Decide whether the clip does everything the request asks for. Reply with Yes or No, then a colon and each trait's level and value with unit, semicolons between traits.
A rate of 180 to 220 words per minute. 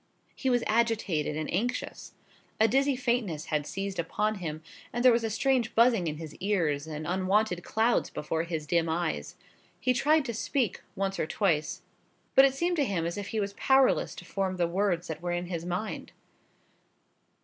Yes: average, 185 wpm